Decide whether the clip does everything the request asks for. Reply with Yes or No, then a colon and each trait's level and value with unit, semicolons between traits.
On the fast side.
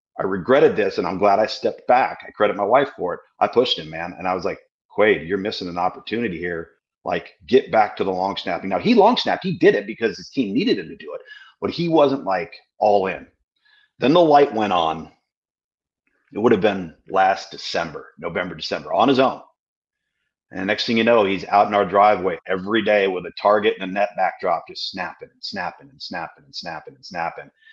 Yes: fast, 225 wpm